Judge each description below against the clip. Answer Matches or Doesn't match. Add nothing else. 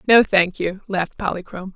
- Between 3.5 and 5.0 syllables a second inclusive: Doesn't match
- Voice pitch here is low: Doesn't match